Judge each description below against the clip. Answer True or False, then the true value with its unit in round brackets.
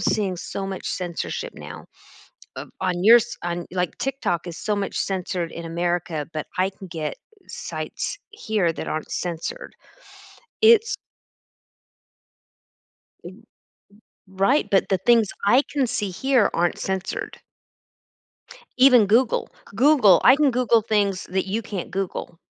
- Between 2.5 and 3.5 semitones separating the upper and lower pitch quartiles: False (5.2 semitones)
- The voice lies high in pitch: True (195 Hz)